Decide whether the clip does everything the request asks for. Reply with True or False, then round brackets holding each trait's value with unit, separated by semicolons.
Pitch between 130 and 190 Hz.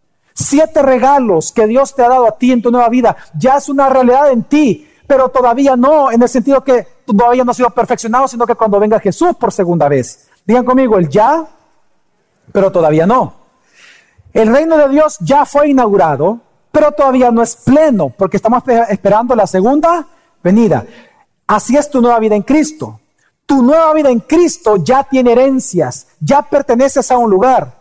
False (250 Hz)